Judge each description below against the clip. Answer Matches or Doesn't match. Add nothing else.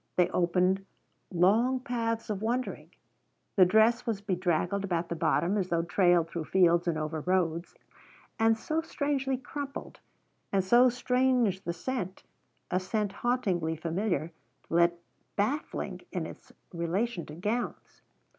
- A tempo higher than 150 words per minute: Doesn't match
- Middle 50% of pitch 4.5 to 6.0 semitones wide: Matches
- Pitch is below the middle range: Doesn't match